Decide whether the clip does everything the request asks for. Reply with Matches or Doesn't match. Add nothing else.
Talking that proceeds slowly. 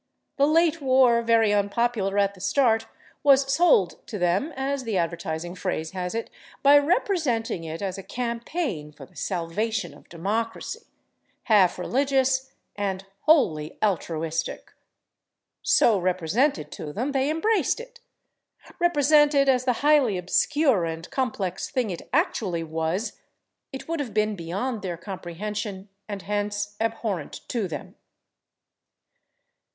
Matches